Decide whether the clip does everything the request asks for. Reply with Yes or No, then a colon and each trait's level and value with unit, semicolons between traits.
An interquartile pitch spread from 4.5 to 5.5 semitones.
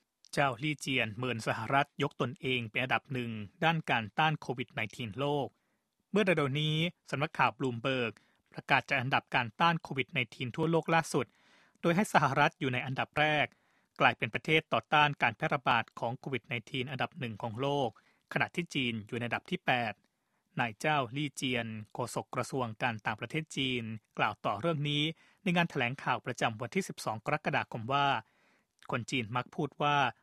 No: average, 4.1 semitones